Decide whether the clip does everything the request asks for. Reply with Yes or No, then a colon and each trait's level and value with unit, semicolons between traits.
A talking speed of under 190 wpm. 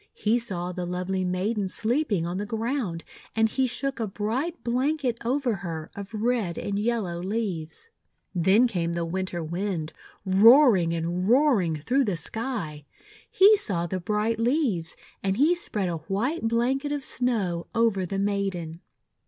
Yes: average, 155 wpm